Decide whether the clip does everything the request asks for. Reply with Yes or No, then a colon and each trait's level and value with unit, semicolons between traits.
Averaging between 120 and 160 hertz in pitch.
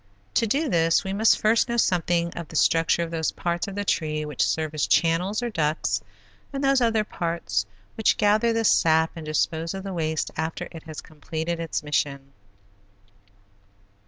No: medium, 170 Hz